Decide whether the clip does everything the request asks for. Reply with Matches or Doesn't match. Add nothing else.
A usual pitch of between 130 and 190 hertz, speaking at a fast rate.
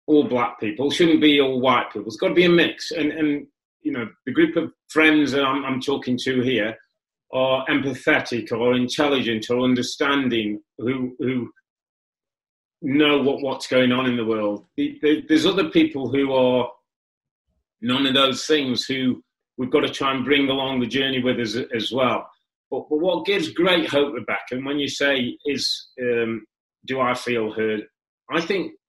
Doesn't match